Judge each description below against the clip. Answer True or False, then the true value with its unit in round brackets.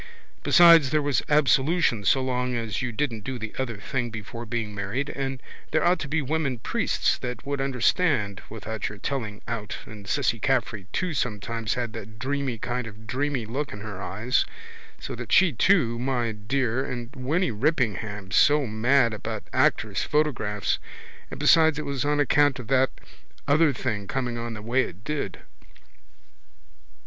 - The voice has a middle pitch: False (125 Hz)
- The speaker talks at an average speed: True (165 wpm)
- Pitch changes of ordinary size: True (4.2 semitones)